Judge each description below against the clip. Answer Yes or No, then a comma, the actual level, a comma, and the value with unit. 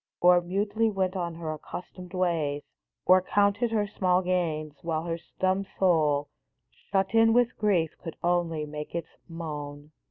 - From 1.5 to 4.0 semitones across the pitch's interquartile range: Yes, average, 3.4 semitones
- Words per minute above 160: No, average, 150 wpm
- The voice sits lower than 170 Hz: No, medium, 175 Hz